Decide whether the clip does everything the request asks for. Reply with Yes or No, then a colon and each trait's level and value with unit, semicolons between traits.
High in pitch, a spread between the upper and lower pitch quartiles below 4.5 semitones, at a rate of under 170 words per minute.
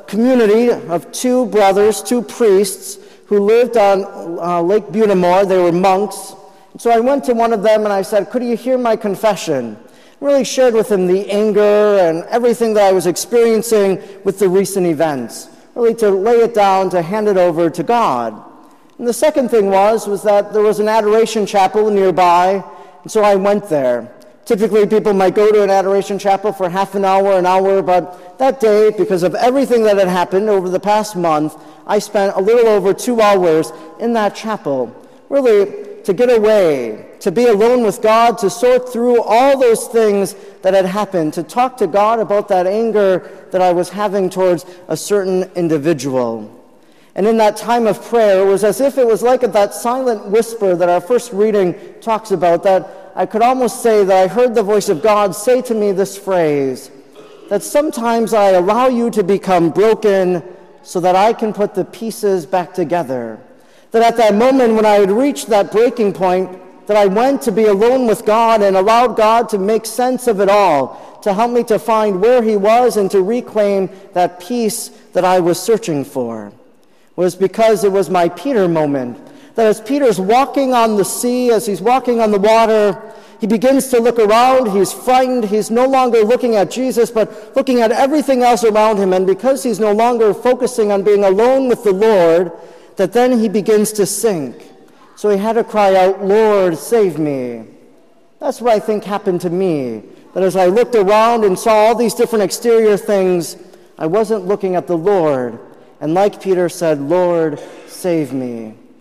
No: high, 210 Hz; average, 3.5 semitones; average, 190 wpm